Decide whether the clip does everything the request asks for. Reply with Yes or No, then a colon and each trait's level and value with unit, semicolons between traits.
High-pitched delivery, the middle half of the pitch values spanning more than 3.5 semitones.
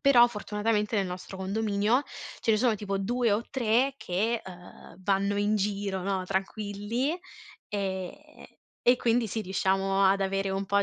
No: high, 205 Hz; average, 2.8 semitones